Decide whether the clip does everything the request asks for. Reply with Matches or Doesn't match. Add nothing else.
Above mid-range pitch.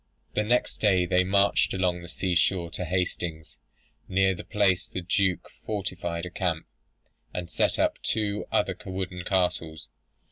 Doesn't match